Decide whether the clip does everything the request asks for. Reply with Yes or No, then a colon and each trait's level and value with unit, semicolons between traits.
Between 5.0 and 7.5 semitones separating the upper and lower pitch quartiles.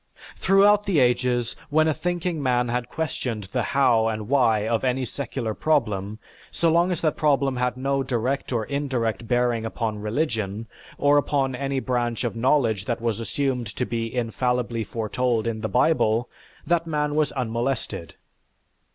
No: average, 3.8 semitones